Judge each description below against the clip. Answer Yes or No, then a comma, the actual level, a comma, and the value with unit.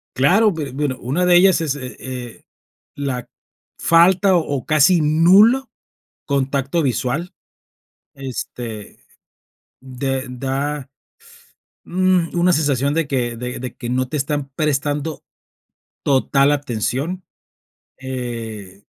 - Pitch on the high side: No, medium, 140 Hz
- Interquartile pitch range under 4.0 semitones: No, average, 4.4 semitones